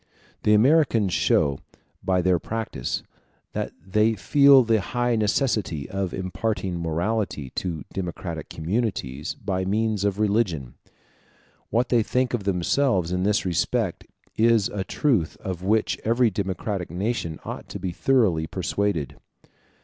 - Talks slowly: Yes, slow, 130 wpm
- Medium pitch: No, low, 100 Hz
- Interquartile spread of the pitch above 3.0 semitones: Yes, average, 4.1 semitones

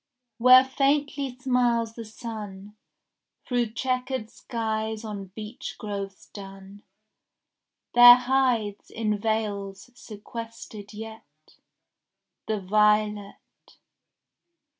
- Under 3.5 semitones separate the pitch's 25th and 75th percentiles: Yes, average, 2.8 semitones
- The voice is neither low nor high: No, high, 220 Hz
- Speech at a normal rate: No, slow, 80 wpm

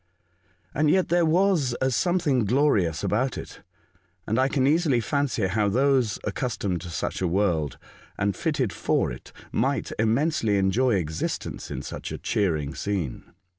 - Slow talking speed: No, average, 155 wpm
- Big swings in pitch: Yes, wide, 6.6 semitones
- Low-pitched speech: Yes, low, 115 Hz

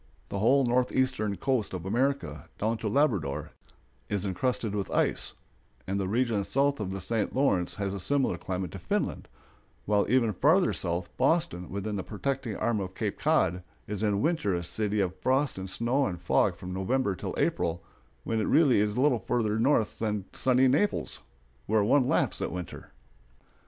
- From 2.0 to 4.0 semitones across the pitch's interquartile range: No, average, 5.3 semitones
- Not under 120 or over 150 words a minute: No, average, 175 wpm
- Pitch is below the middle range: Yes, low, 105 Hz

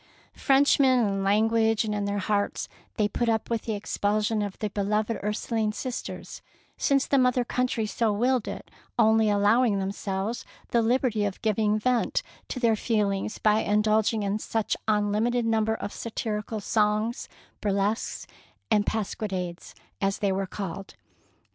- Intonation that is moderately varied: No, narrow, 2.0 semitones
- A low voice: No, high, 215 Hz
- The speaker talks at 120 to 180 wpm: Yes, average, 150 wpm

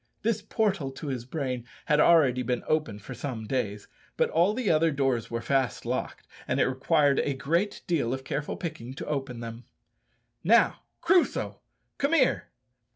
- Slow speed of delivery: No, average, 165 wpm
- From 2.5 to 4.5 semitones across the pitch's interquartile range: No, average, 4.9 semitones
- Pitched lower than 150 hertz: Yes, medium, 140 Hz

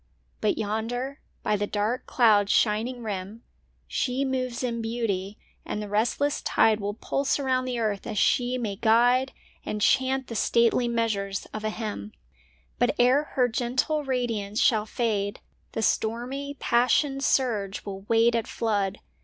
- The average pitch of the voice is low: No, high, 230 Hz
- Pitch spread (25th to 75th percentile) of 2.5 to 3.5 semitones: Yes, average, 3.2 semitones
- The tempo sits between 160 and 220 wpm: No, average, 150 wpm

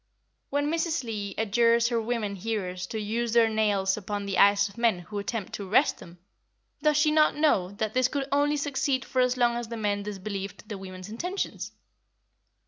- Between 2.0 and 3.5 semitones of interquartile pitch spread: No, average, 4.2 semitones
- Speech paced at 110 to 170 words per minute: No, average, 190 wpm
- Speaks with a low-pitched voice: No, high, 225 Hz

